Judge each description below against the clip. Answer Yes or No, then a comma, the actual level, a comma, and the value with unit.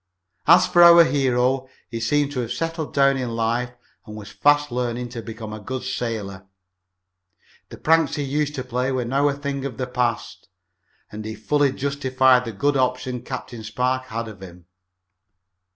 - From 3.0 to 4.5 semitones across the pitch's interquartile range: Yes, average, 3.3 semitones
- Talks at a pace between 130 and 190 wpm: Yes, average, 175 wpm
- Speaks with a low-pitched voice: Yes, low, 125 Hz